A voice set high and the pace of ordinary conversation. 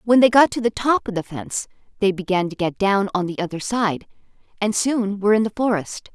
No: high, 205 Hz; fast, 235 wpm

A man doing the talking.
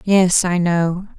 No: female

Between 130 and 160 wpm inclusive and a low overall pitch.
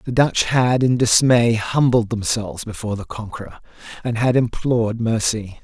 Yes: average, 150 wpm; low, 115 Hz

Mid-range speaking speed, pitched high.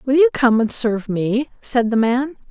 No: fast, 215 wpm; high, 245 Hz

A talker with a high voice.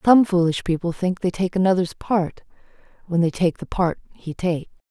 No: medium, 180 Hz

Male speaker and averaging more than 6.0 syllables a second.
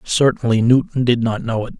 No: male; 5.4 syllables/s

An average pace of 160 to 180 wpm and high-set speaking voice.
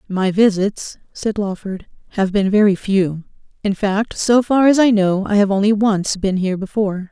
Yes: average, 175 wpm; high, 200 Hz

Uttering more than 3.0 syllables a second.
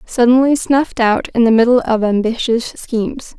Yes: 4.9 syllables/s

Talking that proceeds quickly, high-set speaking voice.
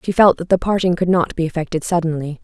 No: fast, 245 wpm; medium, 170 Hz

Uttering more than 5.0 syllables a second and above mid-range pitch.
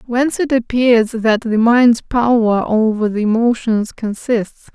No: 3.9 syllables/s; high, 230 Hz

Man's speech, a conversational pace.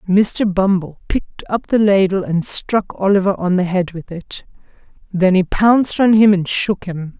No: female; average, 185 wpm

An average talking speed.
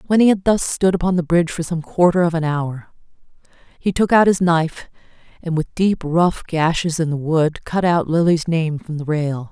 No: fast, 215 wpm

